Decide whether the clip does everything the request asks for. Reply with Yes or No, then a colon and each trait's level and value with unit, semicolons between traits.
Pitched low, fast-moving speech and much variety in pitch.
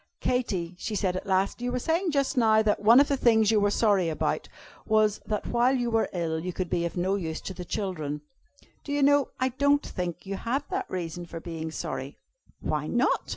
No: high, 210 Hz; fast, 220 wpm; wide, 5.9 semitones